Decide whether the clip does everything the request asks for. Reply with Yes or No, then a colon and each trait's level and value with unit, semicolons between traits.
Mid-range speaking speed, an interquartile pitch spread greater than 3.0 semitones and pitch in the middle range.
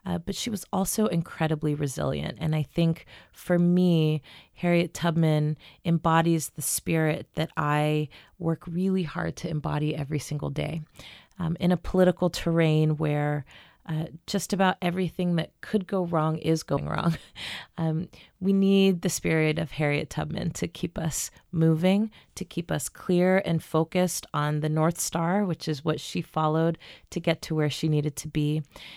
No: average, 165 wpm; narrow, 2.5 semitones; medium, 165 Hz